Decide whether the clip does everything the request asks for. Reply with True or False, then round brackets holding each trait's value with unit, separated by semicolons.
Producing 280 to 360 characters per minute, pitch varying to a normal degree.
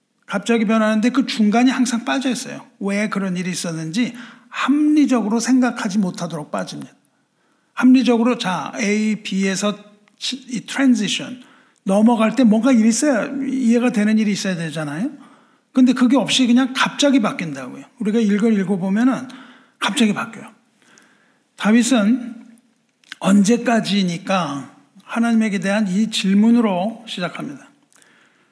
True (300 characters per minute; 3.5 semitones)